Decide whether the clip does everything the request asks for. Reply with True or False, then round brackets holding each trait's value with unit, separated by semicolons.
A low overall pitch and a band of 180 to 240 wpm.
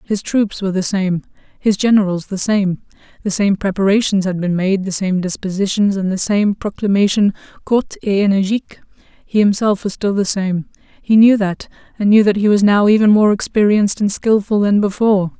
False (200 Hz; 185 wpm)